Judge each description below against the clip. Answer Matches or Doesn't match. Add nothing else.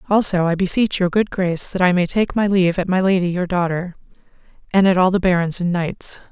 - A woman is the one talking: Matches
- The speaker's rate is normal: Doesn't match